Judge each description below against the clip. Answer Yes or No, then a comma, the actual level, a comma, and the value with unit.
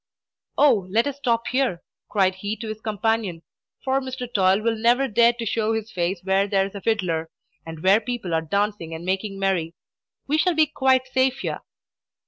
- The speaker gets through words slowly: No, average, 190 wpm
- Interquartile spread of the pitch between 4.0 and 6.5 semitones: Yes, average, 4.4 semitones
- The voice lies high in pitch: Yes, high, 215 Hz